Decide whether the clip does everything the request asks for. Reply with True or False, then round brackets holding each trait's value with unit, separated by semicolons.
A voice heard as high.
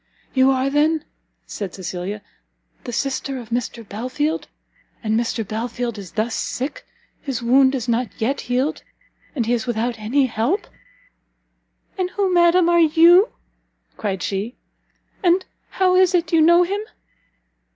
True (260 Hz)